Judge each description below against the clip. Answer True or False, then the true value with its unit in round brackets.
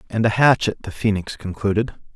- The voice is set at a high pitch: False (105 Hz)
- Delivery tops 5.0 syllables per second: True (5.8 syllables/s)